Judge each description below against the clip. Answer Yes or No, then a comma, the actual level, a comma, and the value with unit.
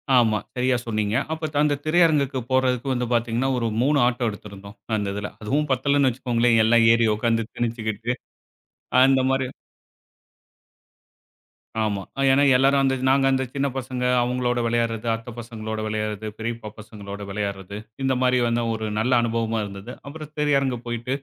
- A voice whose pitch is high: No, low, 120 Hz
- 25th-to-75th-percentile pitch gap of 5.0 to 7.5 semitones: No, average, 3.2 semitones